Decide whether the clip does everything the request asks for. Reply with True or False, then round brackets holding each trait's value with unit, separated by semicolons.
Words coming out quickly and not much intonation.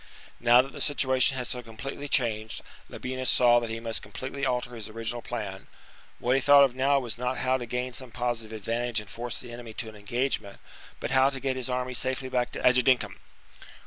True (210 wpm; 2.2 semitones)